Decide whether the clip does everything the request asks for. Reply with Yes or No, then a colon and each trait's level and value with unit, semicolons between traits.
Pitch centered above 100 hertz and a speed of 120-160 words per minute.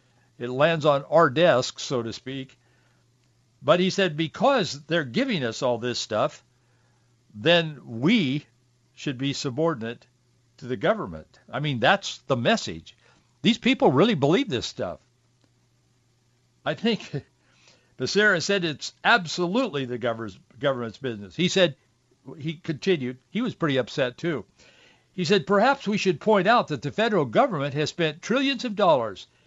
Yes: medium, 140 Hz; average, 145 wpm